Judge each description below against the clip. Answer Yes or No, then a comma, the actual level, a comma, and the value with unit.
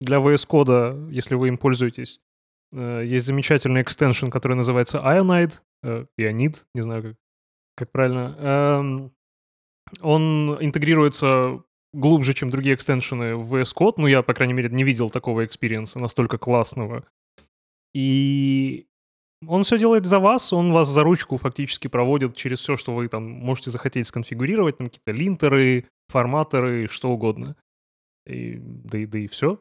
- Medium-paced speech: Yes, average, 145 wpm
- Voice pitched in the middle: No, low, 130 Hz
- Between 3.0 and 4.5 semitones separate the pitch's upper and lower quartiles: Yes, average, 3.6 semitones